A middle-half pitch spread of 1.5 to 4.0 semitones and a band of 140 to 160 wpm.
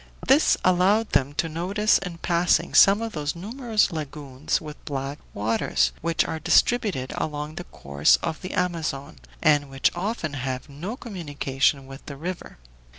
No: average, 4.8 semitones; average, 155 wpm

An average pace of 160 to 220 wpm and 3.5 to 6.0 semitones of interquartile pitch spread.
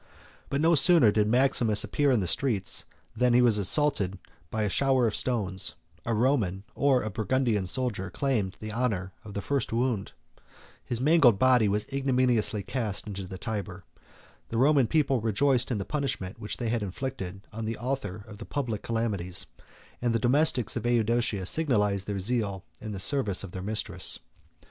Yes: average, 175 wpm; average, 4.3 semitones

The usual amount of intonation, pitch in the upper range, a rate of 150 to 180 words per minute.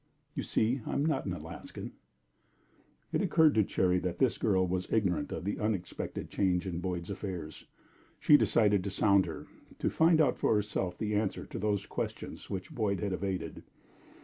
No: average, 3.1 semitones; low, 100 Hz; average, 175 wpm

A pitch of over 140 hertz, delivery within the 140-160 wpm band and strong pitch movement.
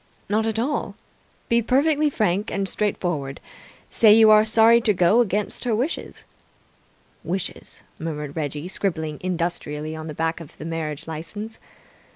Yes: high, 190 Hz; average, 150 wpm; wide, 5.7 semitones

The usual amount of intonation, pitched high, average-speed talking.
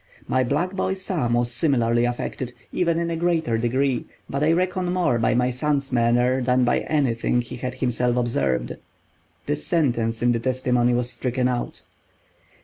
No: average, 3.9 semitones; low, 125 Hz; average, 165 wpm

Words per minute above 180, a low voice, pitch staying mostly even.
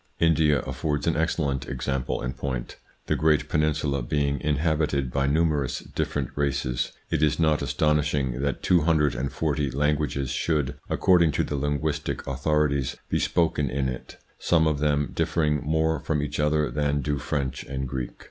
No: average, 165 wpm; very low, 75 Hz; narrow, 2.0 semitones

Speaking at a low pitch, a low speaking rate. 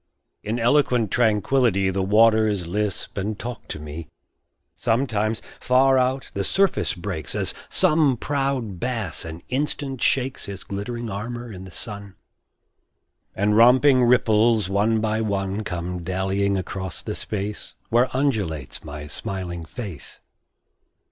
Yes: low, 105 Hz; slow, 130 wpm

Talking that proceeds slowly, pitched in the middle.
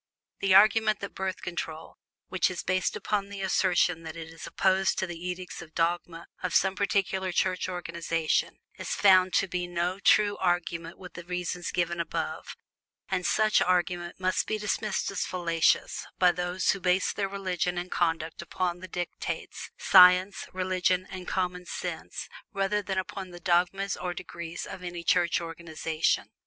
No: average, 165 wpm; medium, 180 Hz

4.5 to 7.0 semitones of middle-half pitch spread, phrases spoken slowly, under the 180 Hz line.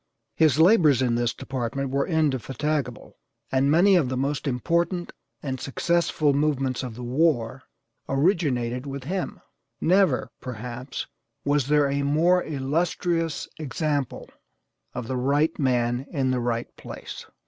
No: average, 3.8 semitones; slow, 130 wpm; medium, 140 Hz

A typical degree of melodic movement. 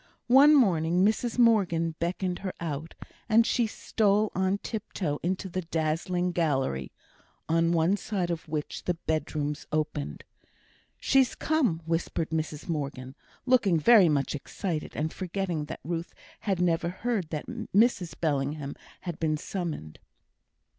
Yes: average, 4.2 semitones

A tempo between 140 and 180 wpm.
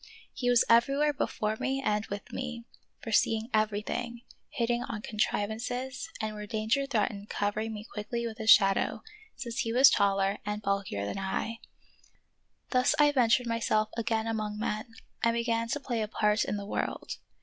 Yes: average, 165 wpm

